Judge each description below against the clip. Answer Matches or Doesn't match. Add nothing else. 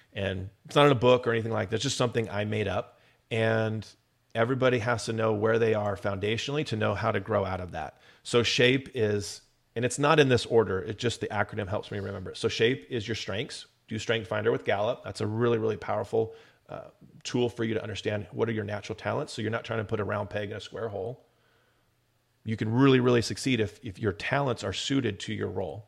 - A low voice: Matches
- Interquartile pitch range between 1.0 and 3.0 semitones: Matches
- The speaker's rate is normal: Doesn't match